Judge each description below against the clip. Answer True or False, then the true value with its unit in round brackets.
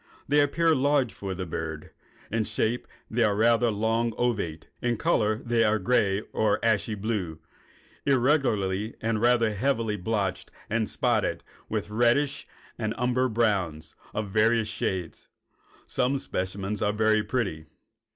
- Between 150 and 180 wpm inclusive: False (140 wpm)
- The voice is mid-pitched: False (110 Hz)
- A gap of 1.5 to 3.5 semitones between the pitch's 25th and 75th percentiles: True (3.1 semitones)